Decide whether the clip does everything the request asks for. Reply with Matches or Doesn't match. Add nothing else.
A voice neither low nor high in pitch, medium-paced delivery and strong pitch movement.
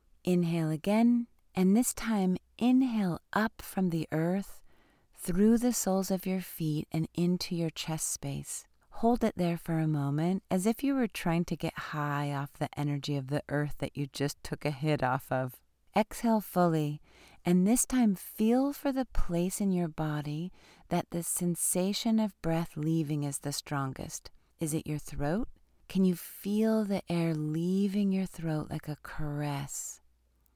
Doesn't match